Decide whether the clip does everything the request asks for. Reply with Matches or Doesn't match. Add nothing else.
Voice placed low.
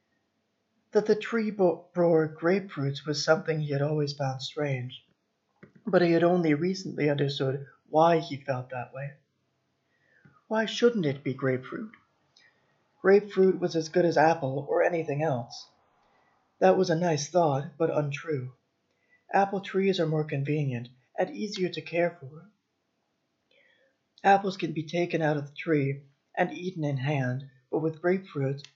Doesn't match